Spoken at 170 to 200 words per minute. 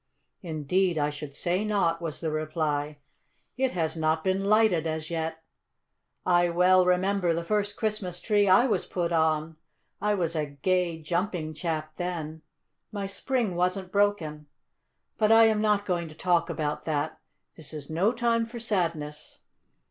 No: average, 155 wpm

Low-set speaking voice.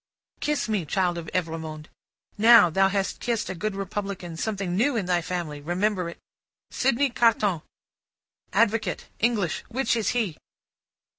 No: high, 195 Hz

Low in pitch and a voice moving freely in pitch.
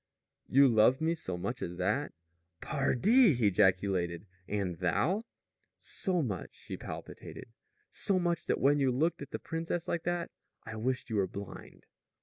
Yes: low, 125 Hz; wide, 8.7 semitones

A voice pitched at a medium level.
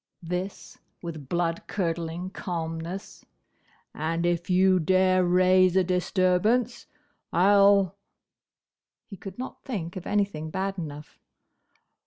Yes: medium, 180 Hz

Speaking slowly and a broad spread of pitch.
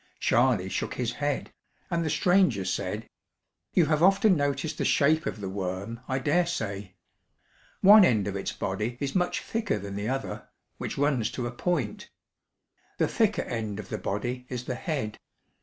No: average, 175 wpm; wide, 6.9 semitones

